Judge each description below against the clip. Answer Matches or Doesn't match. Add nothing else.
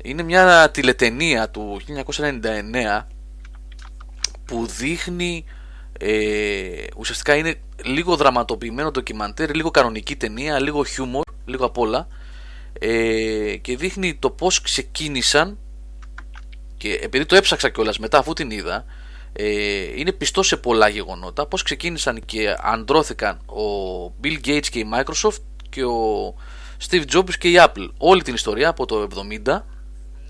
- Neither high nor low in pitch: Doesn't match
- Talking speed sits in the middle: Matches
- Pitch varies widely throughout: Matches